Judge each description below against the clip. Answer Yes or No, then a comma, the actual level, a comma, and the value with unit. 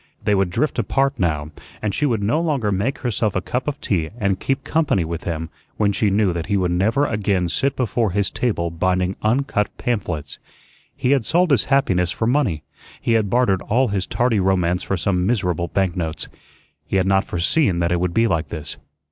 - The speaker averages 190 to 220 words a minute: Yes, average, 200 wpm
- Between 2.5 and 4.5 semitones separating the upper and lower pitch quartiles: No, wide, 5.5 semitones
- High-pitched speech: No, low, 100 Hz